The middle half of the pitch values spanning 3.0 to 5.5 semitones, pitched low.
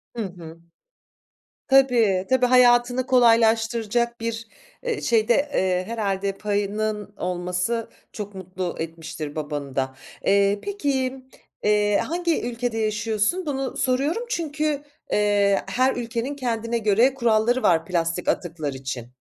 No: average, 4.9 semitones; high, 220 Hz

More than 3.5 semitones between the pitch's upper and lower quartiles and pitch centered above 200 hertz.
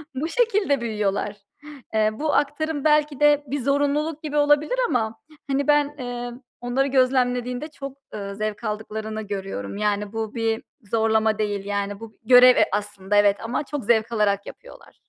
Yes: average, 5.3 semitones; high, 240 Hz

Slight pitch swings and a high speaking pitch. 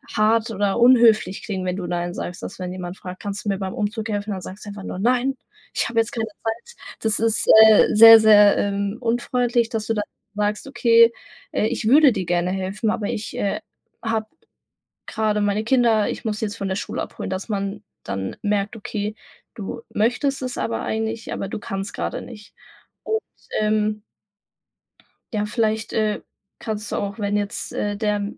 Yes: narrow, 2.1 semitones; high, 210 Hz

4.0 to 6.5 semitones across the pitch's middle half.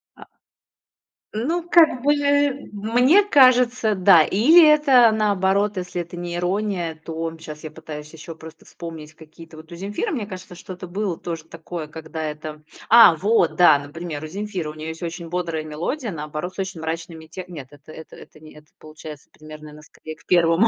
Yes: average, 4.9 semitones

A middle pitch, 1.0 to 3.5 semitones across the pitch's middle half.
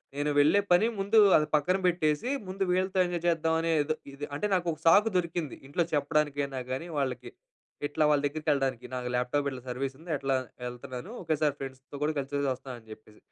No: medium, 150 Hz; average, 4.0 semitones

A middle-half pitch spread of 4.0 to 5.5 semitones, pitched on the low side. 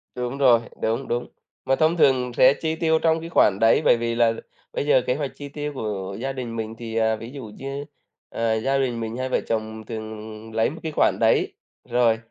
No: average, 3.5 semitones; low, 120 Hz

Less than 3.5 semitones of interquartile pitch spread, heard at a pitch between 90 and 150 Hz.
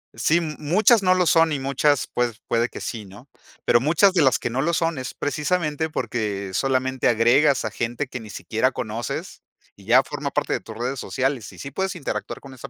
No: average, 4.4 semitones; low, 135 Hz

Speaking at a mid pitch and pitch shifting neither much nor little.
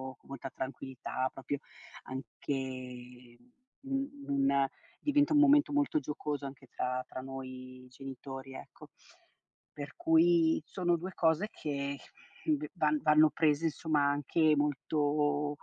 Yes: medium, 145 Hz; average, 3.4 semitones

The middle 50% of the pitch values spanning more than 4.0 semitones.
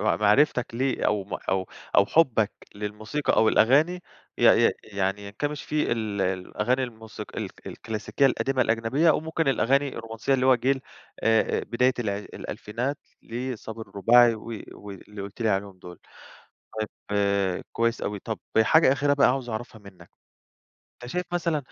Yes: average, 4.6 semitones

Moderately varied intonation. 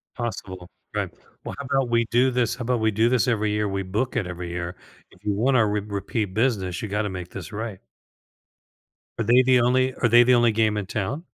Yes: average, 3.6 semitones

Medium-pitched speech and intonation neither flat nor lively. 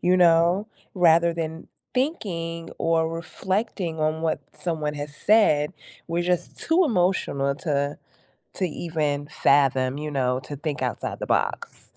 Yes: medium, 165 Hz; average, 3.4 semitones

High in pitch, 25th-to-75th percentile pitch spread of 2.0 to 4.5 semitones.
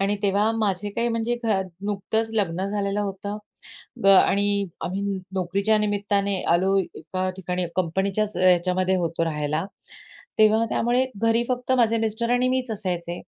Yes: high, 200 Hz; average, 2.9 semitones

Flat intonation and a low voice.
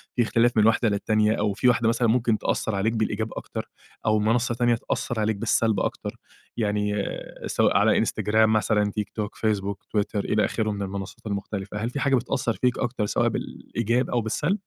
Yes: narrow, 2.1 semitones; low, 110 Hz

